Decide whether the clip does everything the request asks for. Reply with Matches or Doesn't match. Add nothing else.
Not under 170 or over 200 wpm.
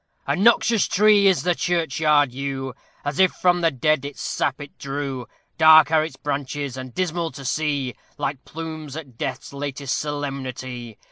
Doesn't match